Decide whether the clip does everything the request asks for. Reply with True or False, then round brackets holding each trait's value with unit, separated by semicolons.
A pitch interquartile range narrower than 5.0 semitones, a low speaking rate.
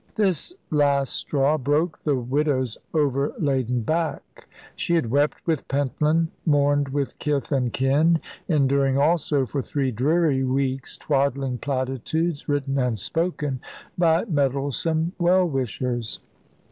True (2.9 semitones; 120 wpm)